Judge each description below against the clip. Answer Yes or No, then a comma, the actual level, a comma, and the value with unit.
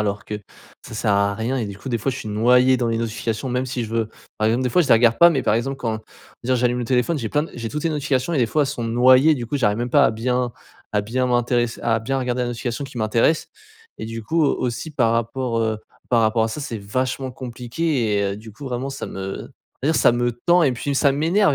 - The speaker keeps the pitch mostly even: No, average, 3.0 semitones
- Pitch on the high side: No, low, 120 Hz